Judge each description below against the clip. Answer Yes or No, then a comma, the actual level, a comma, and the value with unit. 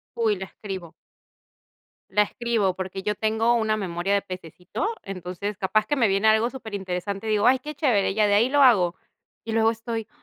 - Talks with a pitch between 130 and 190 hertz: No, high, 210 Hz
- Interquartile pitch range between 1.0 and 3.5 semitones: Yes, average, 2.9 semitones